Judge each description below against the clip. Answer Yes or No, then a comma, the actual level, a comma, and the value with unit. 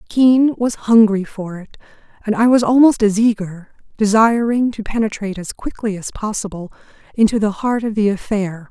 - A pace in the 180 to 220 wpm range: No, average, 165 wpm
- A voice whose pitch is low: No, high, 215 Hz